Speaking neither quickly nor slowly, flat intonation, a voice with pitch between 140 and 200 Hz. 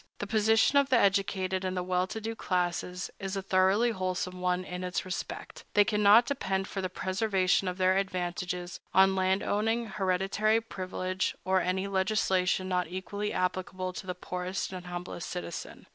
Yes: average, 165 wpm; narrow, 1.7 semitones; high, 190 Hz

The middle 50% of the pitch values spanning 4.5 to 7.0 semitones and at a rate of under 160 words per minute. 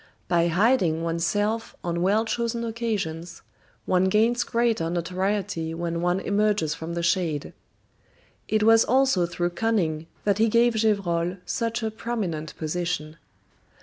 Yes: average, 4.8 semitones; slow, 135 wpm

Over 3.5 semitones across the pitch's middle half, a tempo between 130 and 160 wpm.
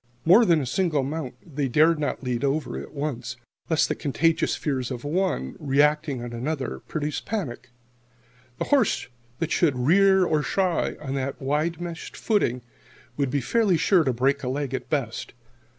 No: average, 4.1 semitones; average, 170 wpm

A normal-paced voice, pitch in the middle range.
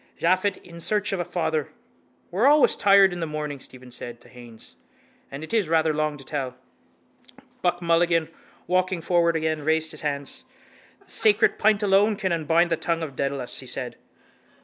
Yes: average, 175 wpm; medium, 165 Hz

